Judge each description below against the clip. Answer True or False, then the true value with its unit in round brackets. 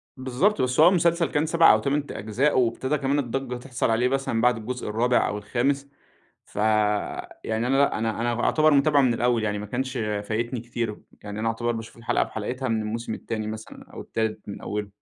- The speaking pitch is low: True (120 Hz)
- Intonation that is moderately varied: True (3.7 semitones)